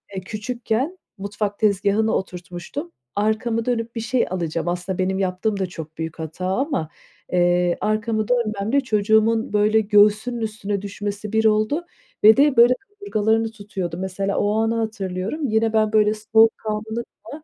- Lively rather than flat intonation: No, average, 2.7 semitones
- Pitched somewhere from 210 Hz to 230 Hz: Yes, high, 215 Hz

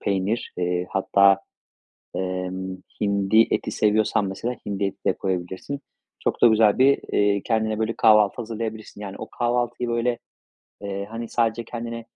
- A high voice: No, low, 105 Hz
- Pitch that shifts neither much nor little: Yes, average, 3.0 semitones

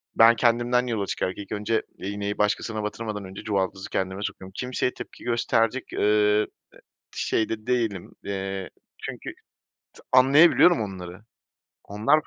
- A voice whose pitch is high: No, low, 105 Hz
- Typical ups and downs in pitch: Yes, average, 3.1 semitones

